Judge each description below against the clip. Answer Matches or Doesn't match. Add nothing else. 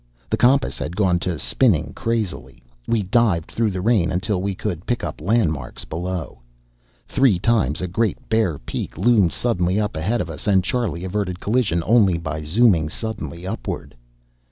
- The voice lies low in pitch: Matches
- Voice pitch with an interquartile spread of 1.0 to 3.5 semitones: Doesn't match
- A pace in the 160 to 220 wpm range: Matches